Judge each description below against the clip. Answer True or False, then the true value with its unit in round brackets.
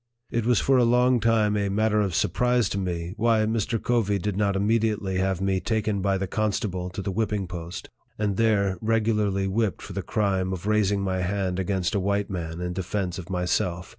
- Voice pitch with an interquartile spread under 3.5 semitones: True (2.6 semitones)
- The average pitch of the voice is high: False (100 Hz)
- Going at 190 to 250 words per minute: True (200 wpm)